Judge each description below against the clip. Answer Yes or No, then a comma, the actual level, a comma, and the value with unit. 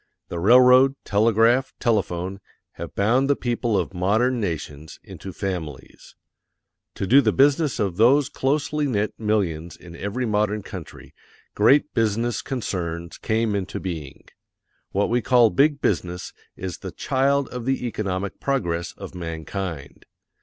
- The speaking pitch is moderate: No, low, 105 Hz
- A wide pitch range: Yes, wide, 5.8 semitones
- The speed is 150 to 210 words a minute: No, slow, 135 wpm